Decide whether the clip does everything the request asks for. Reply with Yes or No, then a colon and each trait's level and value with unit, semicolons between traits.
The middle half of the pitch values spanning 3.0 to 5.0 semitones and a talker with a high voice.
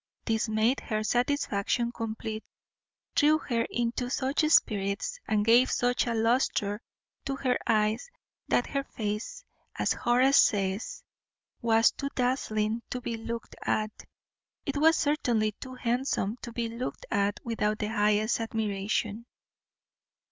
No: narrow, 2.6 semitones; high, 230 Hz